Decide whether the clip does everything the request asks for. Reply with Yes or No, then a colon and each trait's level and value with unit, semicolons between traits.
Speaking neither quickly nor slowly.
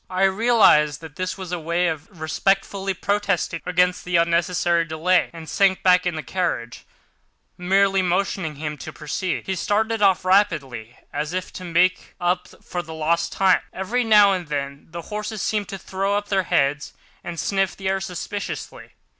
Yes: average, 170 wpm